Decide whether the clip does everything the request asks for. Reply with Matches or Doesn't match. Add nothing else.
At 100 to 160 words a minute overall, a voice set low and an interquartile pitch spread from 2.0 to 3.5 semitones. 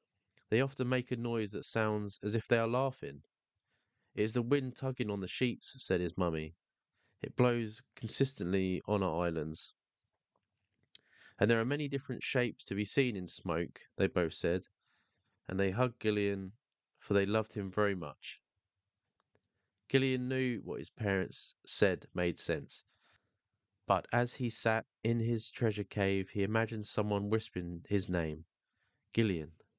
Doesn't match